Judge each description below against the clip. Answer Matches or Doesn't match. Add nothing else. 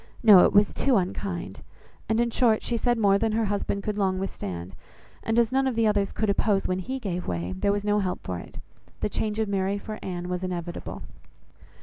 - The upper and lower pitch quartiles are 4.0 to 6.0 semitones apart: Doesn't match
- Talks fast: Matches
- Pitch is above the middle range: Matches